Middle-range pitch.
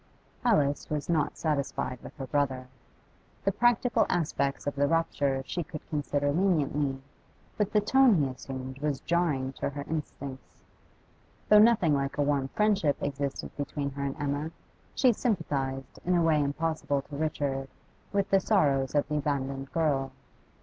Yes: medium, 145 Hz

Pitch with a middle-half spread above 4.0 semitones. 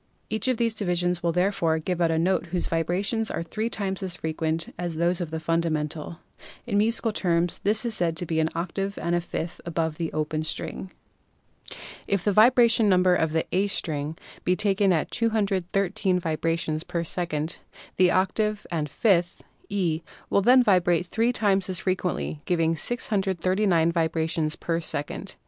No: average, 3.3 semitones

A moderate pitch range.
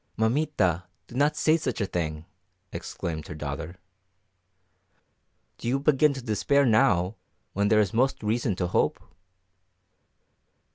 No: wide, 7.2 semitones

